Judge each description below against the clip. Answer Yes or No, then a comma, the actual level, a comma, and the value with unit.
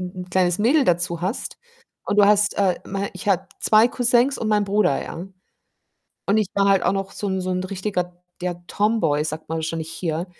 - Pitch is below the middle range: No, high, 190 Hz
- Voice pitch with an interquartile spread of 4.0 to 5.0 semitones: No, average, 2.9 semitones